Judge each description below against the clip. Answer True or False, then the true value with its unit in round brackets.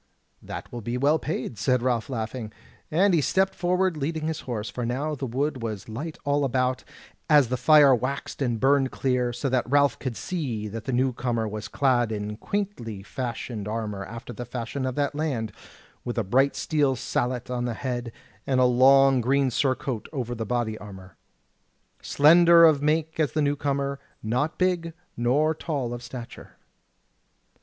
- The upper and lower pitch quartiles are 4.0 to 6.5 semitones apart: False (3.6 semitones)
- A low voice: True (130 Hz)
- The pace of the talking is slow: False (175 wpm)